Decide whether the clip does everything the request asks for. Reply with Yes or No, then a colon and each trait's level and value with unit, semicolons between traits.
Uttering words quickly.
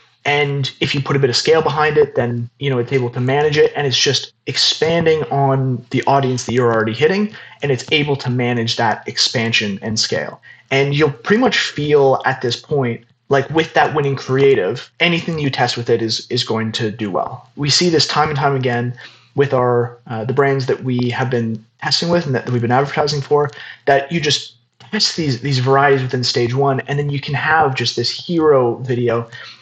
Yes: fast, 215 wpm